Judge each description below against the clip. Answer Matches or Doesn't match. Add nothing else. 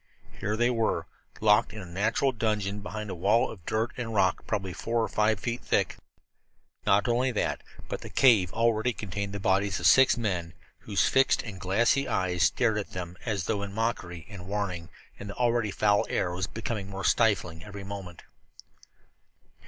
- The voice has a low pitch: Matches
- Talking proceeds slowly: Doesn't match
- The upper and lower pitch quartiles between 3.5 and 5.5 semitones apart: Doesn't match